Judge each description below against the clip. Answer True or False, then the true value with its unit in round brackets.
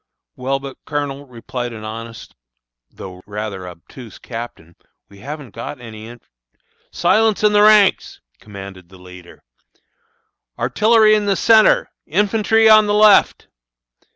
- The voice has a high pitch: False (125 Hz)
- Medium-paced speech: False (130 wpm)